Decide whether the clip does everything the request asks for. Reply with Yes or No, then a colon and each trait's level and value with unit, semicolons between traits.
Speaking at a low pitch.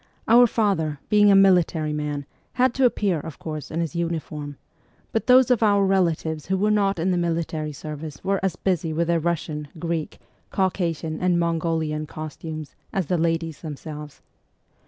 No: medium, 165 Hz